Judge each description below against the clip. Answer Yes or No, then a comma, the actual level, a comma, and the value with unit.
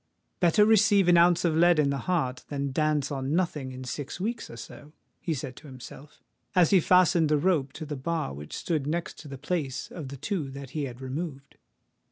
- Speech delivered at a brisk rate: Yes, fast, 215 wpm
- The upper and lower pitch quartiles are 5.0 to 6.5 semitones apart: No, average, 4.2 semitones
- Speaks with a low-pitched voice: No, medium, 150 Hz